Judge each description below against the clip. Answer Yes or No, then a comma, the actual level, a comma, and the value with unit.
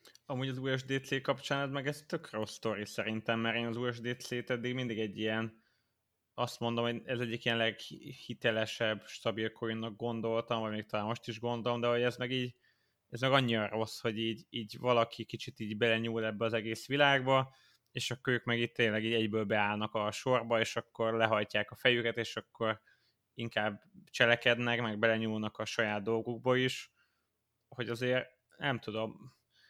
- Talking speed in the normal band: No, fast, 170 wpm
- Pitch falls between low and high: No, low, 115 Hz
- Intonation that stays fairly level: Yes, narrow, 2.0 semitones